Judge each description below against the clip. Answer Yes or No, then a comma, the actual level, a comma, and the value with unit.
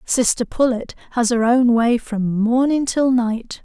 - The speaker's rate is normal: Yes, average, 165 wpm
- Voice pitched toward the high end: Yes, high, 240 Hz